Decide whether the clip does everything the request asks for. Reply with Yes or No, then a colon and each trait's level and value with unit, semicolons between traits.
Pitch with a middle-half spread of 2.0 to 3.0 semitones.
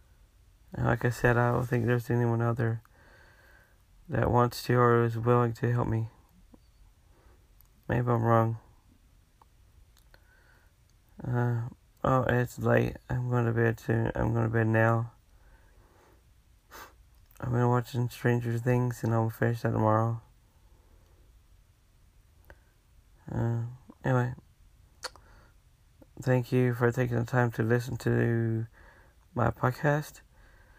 No: average, 3.9 semitones